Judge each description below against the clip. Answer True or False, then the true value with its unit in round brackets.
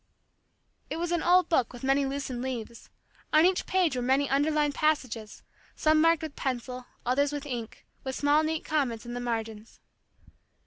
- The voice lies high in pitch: True (275 Hz)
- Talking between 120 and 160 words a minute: False (170 wpm)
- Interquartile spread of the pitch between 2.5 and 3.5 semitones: False (4.1 semitones)